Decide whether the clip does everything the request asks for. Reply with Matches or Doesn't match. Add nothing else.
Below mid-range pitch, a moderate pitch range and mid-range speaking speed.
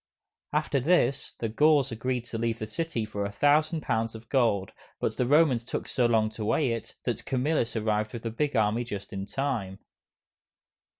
Matches